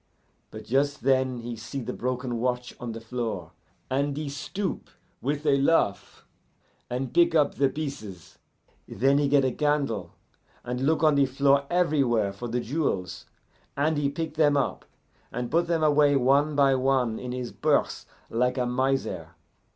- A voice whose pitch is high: No, low, 135 Hz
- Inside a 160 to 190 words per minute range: Yes, average, 165 wpm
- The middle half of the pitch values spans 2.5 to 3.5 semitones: Yes, average, 3.0 semitones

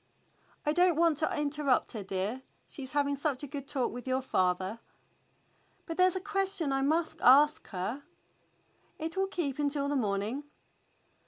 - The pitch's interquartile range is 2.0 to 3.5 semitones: No, average, 4.0 semitones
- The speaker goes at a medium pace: Yes, average, 165 wpm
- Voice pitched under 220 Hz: No, very high, 285 Hz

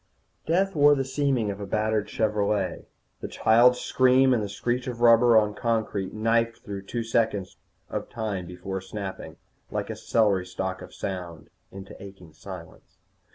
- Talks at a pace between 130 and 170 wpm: Yes, average, 160 wpm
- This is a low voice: Yes, low, 105 Hz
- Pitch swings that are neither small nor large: Yes, average, 3.7 semitones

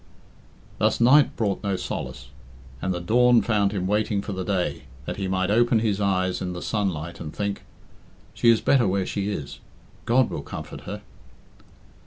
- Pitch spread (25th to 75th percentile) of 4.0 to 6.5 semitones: No, average, 3.1 semitones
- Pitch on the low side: Yes, low, 100 Hz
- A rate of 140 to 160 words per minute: No, average, 175 wpm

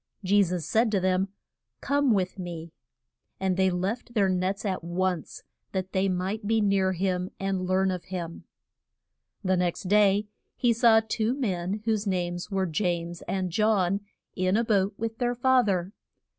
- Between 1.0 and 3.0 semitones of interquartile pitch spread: Yes, average, 2.7 semitones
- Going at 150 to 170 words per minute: Yes, average, 165 wpm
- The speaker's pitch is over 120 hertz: Yes, high, 190 Hz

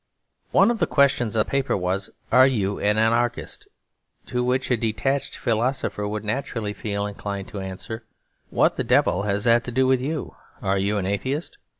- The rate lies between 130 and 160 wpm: No, average, 185 wpm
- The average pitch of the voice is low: Yes, low, 110 Hz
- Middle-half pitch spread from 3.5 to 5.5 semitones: Yes, average, 4.2 semitones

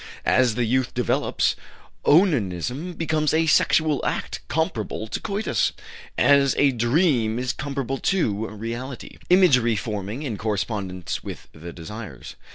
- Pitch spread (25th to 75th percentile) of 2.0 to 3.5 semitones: No, wide, 5.5 semitones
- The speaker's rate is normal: No, slow, 125 wpm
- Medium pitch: No, low, 125 Hz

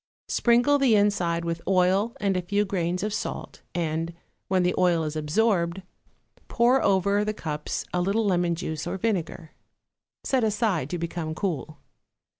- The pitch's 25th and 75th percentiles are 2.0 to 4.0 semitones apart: Yes, average, 3.7 semitones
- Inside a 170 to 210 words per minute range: No, average, 155 wpm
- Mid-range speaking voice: Yes, medium, 180 Hz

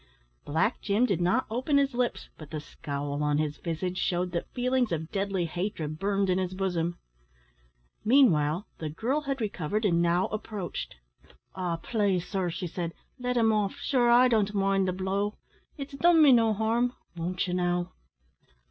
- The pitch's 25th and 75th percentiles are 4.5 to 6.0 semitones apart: Yes, average, 4.9 semitones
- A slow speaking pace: No, average, 170 wpm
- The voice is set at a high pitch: Yes, high, 195 Hz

